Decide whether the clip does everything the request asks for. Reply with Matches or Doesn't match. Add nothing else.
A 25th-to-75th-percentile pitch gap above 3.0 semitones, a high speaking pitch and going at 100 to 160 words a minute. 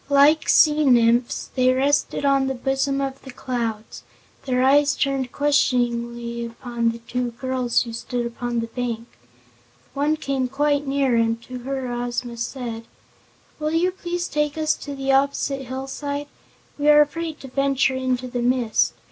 Doesn't match